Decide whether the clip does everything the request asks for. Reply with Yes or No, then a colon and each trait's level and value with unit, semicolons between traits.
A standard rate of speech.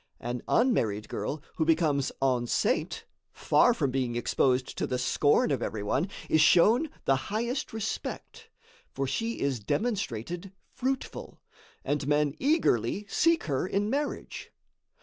No: slow, 130 wpm